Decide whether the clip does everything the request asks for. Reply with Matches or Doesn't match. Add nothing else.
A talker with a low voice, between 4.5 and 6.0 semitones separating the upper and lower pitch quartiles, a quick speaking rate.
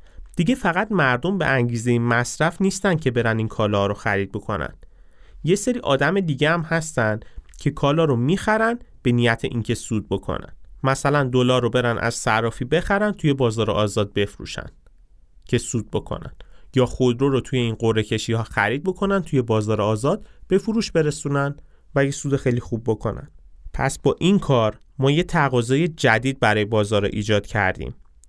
Matches